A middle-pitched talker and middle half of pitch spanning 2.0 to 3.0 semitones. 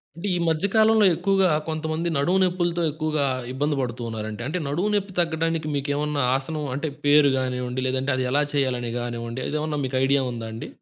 No: medium, 150 Hz; average, 4.1 semitones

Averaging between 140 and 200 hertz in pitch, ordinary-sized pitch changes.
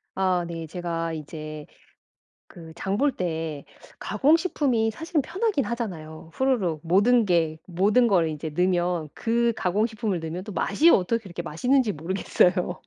No: medium, 185 Hz; wide, 6.0 semitones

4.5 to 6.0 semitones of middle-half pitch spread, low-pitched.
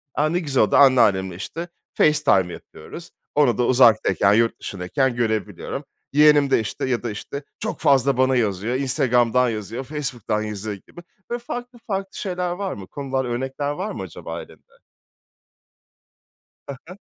Yes: average, 5.3 semitones; low, 130 Hz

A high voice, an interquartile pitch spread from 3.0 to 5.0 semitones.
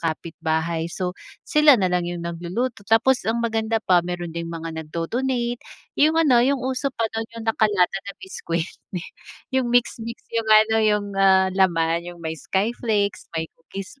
No: high, 200 Hz; wide, 5.5 semitones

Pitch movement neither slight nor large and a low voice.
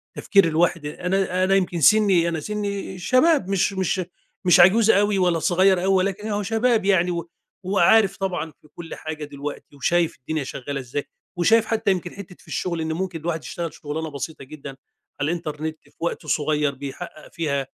No: average, 3.9 semitones; medium, 175 Hz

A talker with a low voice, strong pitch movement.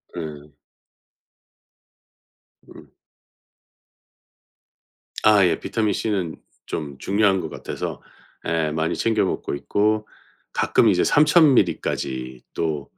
Yes: very low, 90 Hz; wide, 5.8 semitones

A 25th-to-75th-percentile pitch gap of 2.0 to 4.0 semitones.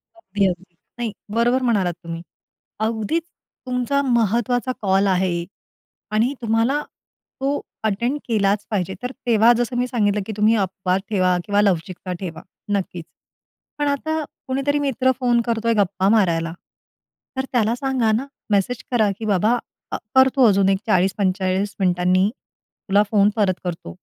No: average, 4.4 semitones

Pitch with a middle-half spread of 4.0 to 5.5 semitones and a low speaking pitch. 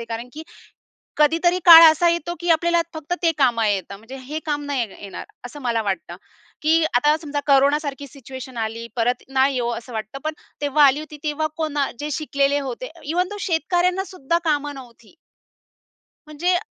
No: average, 4.3 semitones; very high, 290 Hz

